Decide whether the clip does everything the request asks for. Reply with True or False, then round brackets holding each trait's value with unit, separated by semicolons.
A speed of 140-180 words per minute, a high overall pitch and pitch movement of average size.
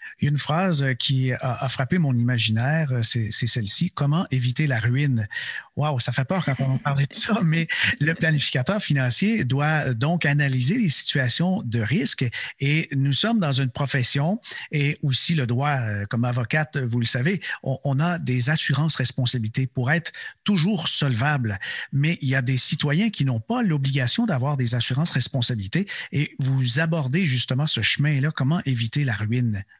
False (170 wpm; 140 Hz; 4.0 semitones)